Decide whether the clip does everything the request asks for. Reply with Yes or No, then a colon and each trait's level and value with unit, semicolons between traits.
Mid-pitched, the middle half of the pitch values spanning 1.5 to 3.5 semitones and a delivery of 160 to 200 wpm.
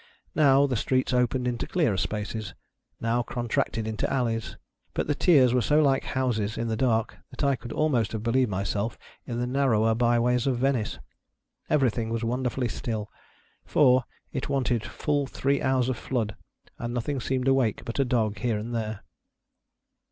No: low, 120 Hz; average, 2.8 semitones; average, 170 wpm